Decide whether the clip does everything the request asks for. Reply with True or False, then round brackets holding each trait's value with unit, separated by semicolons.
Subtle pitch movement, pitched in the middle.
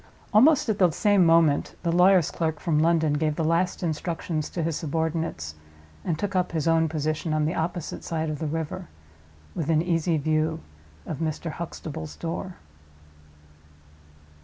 True (1.8 semitones; 165 Hz)